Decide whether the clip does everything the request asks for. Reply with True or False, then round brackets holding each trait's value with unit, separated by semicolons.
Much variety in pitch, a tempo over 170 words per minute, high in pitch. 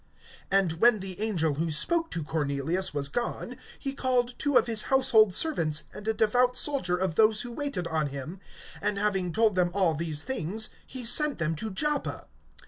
True (6.9 semitones; 185 wpm; 200 Hz)